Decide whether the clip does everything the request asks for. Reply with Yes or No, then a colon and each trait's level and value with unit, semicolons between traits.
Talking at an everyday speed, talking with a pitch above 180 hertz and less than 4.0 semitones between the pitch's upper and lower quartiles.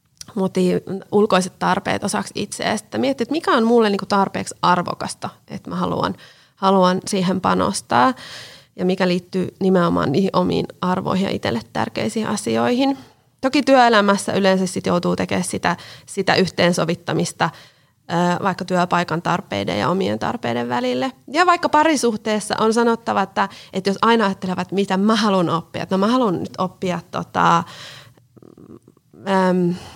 Yes: average, 135 wpm; high, 190 Hz; average, 3.5 semitones